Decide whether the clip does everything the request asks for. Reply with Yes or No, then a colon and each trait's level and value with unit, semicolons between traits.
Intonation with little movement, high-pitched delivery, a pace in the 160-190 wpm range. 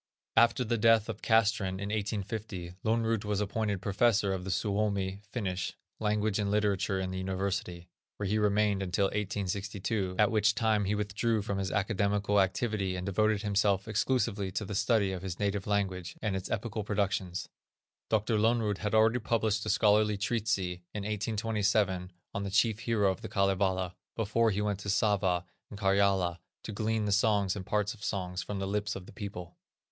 No: narrow, 2.0 semitones; low, 100 Hz; average, 175 wpm